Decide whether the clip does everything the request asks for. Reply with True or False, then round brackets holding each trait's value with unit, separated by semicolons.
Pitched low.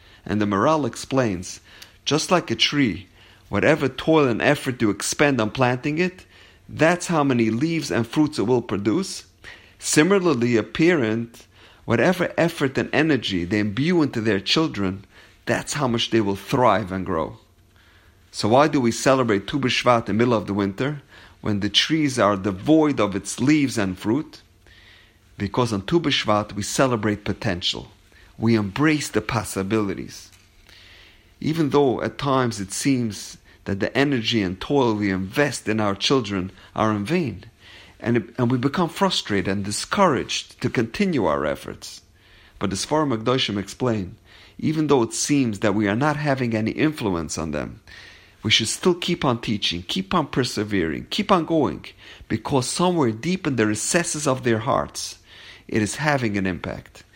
True (110 Hz)